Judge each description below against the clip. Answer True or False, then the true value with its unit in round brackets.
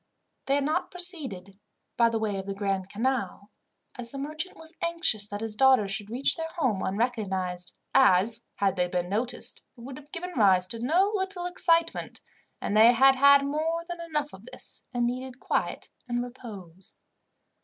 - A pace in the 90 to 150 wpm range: False (175 wpm)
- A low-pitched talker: False (245 Hz)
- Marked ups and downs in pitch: True (6.6 semitones)